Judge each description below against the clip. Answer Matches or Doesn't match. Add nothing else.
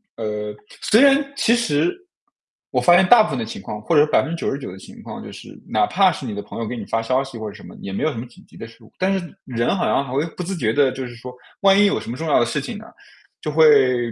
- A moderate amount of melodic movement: Doesn't match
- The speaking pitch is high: Doesn't match